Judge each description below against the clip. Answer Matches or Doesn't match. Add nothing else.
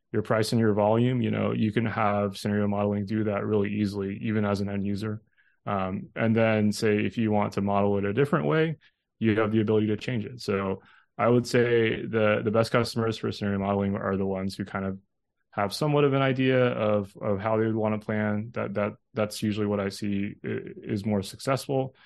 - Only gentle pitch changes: Matches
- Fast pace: Matches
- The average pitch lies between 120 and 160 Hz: Doesn't match